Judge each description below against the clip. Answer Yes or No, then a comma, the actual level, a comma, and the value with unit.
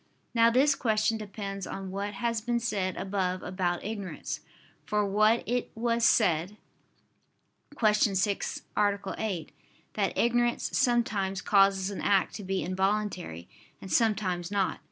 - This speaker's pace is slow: Yes, slow, 130 wpm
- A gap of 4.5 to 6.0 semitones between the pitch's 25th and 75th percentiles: No, average, 2.7 semitones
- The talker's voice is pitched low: No, high, 205 Hz